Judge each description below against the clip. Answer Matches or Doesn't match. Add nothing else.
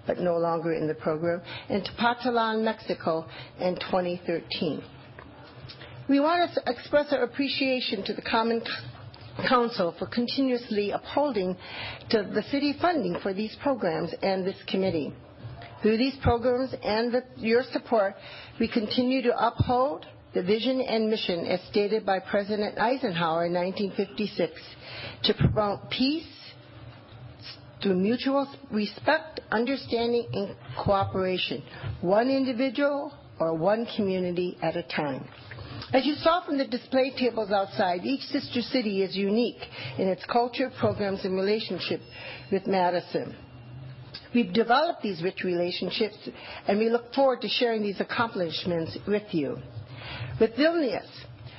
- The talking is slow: Matches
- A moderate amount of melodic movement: Doesn't match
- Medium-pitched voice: Doesn't match